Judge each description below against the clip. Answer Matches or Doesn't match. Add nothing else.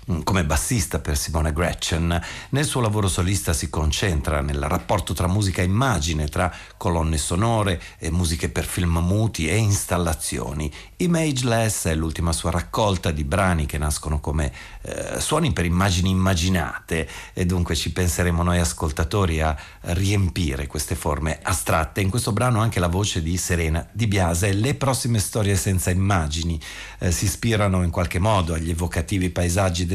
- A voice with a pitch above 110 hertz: Doesn't match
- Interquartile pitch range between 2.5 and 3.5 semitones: Matches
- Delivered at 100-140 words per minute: Doesn't match